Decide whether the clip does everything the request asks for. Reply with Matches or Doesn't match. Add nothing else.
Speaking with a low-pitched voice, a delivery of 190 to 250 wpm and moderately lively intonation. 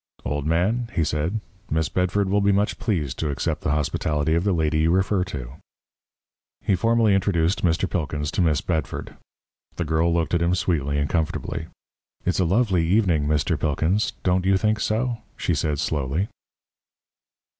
Doesn't match